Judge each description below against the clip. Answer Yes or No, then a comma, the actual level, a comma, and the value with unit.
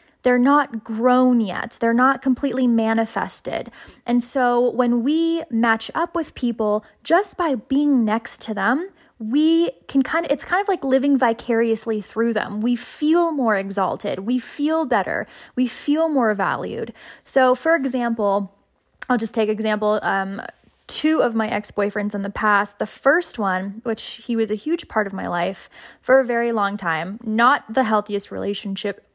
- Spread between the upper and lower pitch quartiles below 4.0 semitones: No, average, 4.4 semitones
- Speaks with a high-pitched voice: Yes, high, 240 Hz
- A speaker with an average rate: Yes, average, 165 wpm